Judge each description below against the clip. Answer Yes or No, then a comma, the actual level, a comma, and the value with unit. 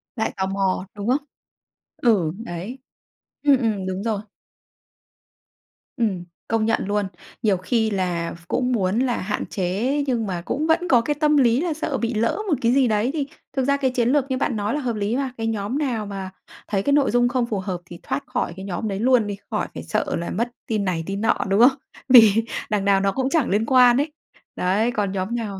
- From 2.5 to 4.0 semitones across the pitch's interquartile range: No, average, 4.6 semitones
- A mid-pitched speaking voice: No, high, 225 Hz